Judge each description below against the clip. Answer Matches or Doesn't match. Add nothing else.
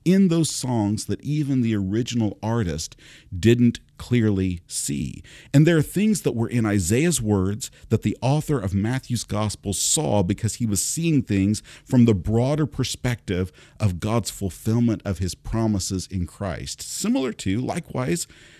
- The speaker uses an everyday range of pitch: Matches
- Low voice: Matches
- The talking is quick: Doesn't match